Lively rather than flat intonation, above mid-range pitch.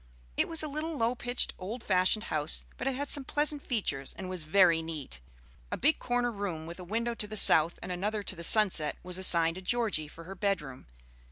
Yes: wide, 6.3 semitones; high, 195 Hz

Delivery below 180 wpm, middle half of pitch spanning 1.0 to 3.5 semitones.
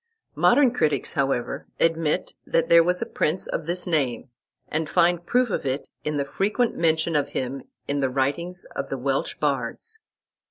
No: average, 170 wpm; average, 4.1 semitones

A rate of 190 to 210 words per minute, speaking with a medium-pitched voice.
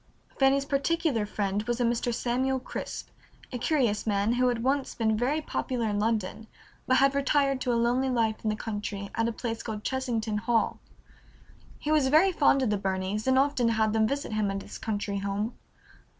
No: average, 195 wpm; high, 235 Hz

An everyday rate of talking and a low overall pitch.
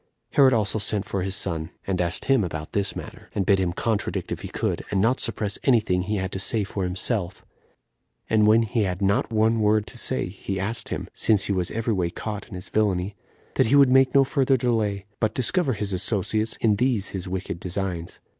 No: fast, 220 wpm; low, 105 Hz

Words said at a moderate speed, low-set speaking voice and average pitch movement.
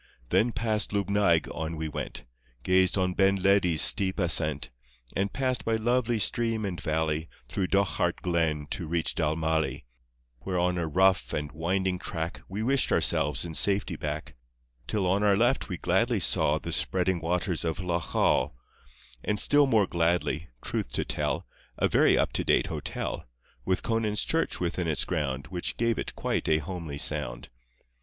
Yes: average, 165 wpm; very low, 90 Hz; average, 4.0 semitones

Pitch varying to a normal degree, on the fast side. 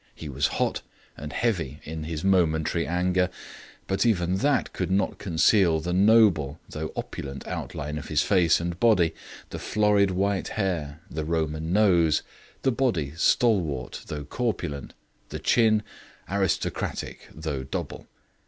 No: average, 4.3 semitones; slow, 135 wpm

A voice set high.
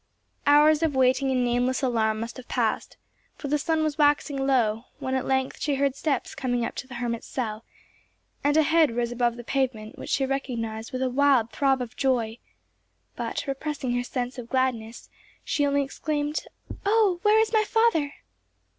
Yes: very high, 265 Hz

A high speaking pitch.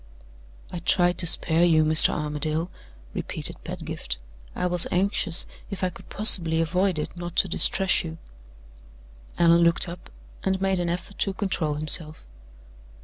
No: medium, 175 Hz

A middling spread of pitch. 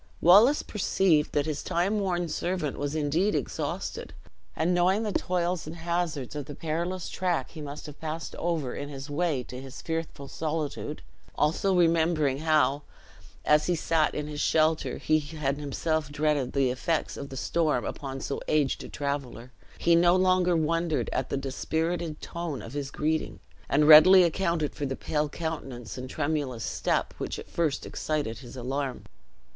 Yes: average, 3.1 semitones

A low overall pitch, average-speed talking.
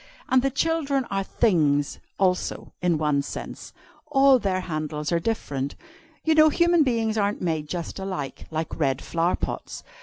No: medium, 185 Hz; average, 155 wpm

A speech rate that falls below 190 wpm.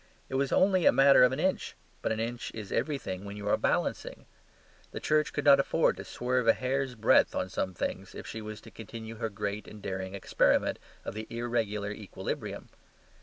No: average, 200 wpm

